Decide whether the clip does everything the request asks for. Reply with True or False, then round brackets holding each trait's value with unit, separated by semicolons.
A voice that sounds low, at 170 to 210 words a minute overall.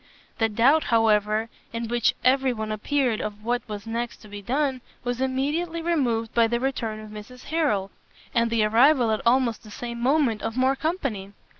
False (235 Hz; 180 wpm)